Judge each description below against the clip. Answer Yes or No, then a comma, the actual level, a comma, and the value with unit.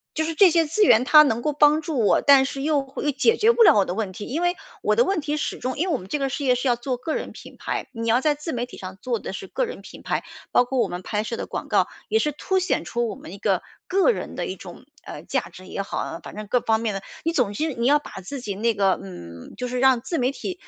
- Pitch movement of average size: No, wide, 5.8 semitones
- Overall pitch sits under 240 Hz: No, very high, 260 Hz